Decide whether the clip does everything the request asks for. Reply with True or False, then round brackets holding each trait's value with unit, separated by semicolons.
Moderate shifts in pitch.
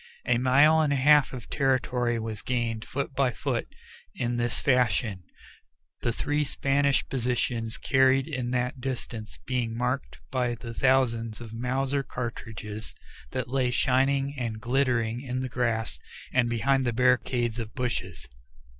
False (2.3 semitones)